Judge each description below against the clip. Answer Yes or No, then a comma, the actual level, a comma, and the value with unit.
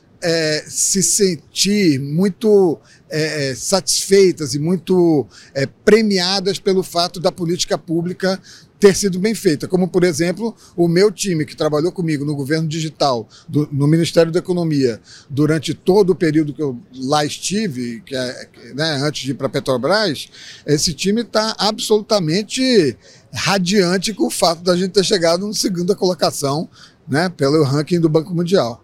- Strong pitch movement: No, average, 4.4 semitones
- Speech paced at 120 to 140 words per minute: No, average, 155 wpm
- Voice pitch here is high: No, medium, 170 Hz